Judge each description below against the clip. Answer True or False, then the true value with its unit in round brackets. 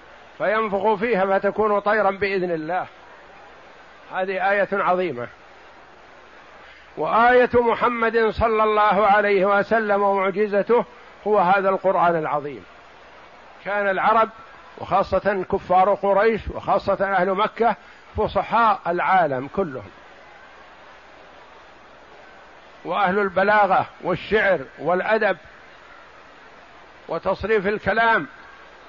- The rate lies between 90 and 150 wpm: False (80 wpm)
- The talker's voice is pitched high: True (200 Hz)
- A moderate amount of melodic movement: False (2.2 semitones)